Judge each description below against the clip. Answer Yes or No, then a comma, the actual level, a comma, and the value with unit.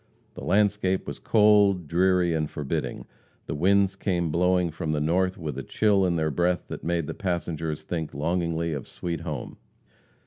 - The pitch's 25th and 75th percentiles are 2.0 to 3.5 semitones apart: Yes, average, 2.9 semitones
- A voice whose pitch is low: Yes, very low, 85 Hz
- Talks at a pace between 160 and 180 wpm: Yes, average, 170 wpm